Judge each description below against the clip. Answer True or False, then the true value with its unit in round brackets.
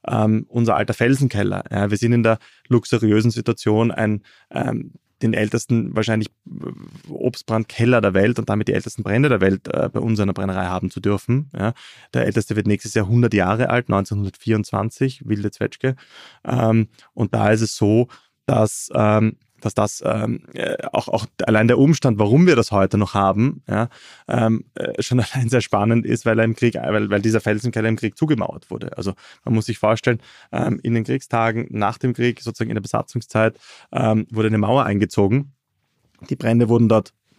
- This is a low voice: True (110 Hz)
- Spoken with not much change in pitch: True (2.3 semitones)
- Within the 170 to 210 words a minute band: True (180 wpm)